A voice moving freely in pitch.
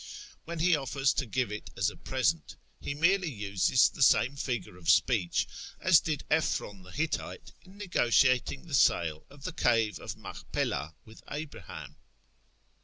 Yes: wide, 7.1 semitones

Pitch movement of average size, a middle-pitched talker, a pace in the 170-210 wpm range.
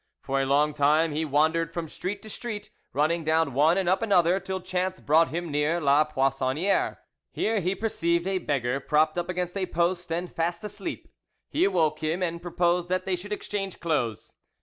Yes: average, 3.4 semitones; medium, 170 Hz; average, 185 wpm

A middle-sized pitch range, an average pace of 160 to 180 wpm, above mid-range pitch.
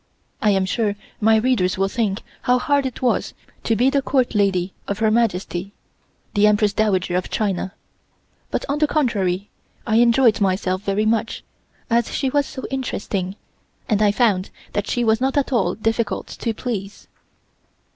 Yes: average, 3.8 semitones; average, 165 wpm; high, 215 Hz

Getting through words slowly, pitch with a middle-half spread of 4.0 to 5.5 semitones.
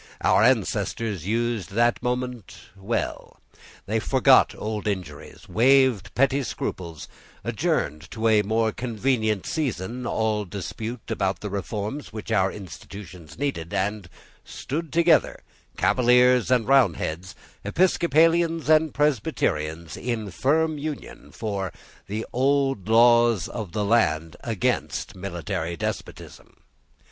Yes: slow, 110 wpm; average, 4.7 semitones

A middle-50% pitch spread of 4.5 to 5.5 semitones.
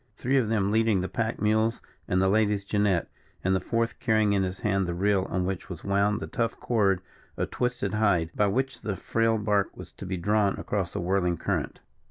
No: narrow, 2.5 semitones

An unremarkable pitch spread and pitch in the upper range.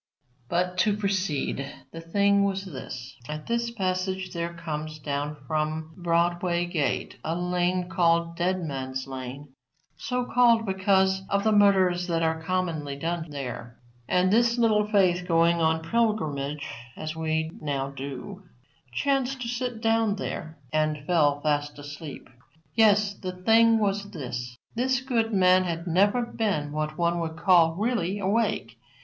No: average, 4.7 semitones; medium, 175 Hz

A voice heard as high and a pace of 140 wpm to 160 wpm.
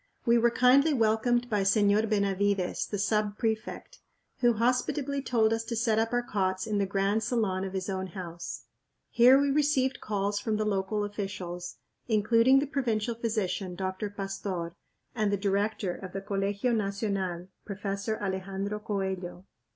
Yes: high, 205 Hz; average, 155 wpm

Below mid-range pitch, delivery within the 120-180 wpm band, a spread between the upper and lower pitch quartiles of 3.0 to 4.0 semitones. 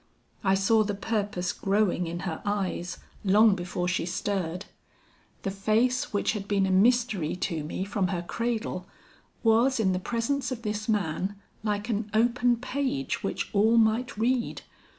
No: high, 205 Hz; average, 155 wpm; average, 3.5 semitones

